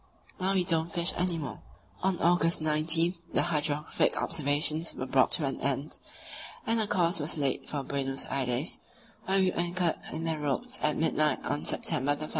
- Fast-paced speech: No, average, 175 wpm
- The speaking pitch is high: No, medium, 160 Hz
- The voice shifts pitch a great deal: No, average, 3.3 semitones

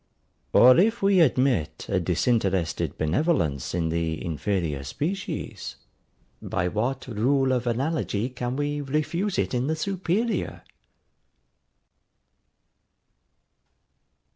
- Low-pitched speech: Yes, low, 125 Hz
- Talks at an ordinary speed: No, slow, 95 wpm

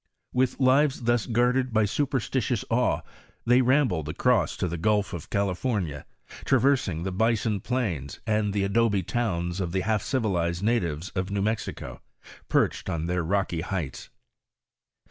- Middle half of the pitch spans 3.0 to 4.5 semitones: No, wide, 5.5 semitones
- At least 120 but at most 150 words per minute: Yes, average, 145 wpm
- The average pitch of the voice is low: Yes, low, 105 Hz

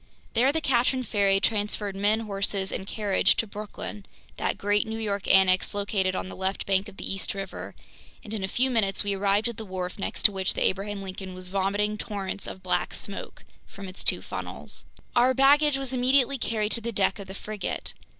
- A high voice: Yes, high, 205 Hz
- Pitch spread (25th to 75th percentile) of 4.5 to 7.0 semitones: No, narrow, 2.6 semitones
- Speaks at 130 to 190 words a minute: No, fast, 205 wpm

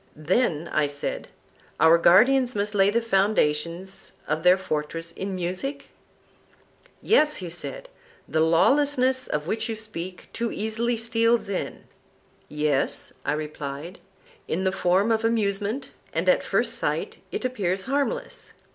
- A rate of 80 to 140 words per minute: Yes, slow, 135 wpm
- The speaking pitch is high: Yes, high, 195 Hz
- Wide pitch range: Yes, wide, 5.7 semitones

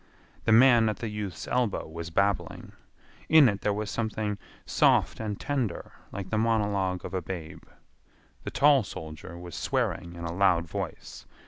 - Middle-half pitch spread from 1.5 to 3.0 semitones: No, average, 4.3 semitones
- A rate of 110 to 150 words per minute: No, average, 160 wpm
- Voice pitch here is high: No, low, 100 Hz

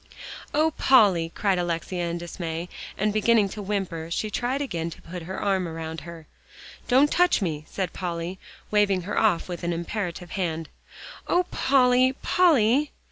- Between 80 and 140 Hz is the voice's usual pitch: No, high, 190 Hz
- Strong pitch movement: No, average, 5.0 semitones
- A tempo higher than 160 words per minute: No, average, 155 wpm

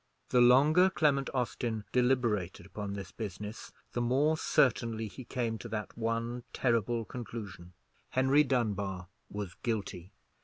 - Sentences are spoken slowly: Yes, slow, 125 wpm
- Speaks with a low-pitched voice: Yes, low, 115 Hz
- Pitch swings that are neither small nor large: Yes, average, 3.5 semitones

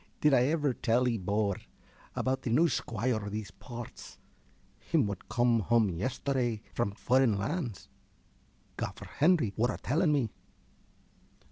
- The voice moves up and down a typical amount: Yes, average, 3.8 semitones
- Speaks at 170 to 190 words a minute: No, average, 145 wpm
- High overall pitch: No, low, 120 Hz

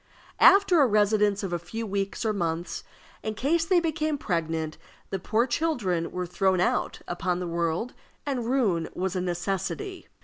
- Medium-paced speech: Yes, average, 165 wpm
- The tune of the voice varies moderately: No, wide, 6.6 semitones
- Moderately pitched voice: No, high, 200 Hz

